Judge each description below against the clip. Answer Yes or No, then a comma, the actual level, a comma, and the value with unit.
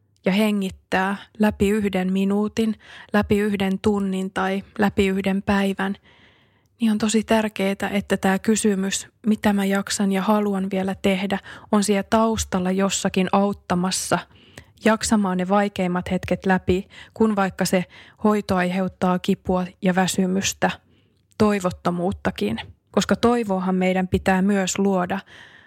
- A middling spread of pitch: No, narrow, 1.7 semitones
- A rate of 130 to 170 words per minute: No, average, 120 wpm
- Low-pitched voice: No, high, 195 Hz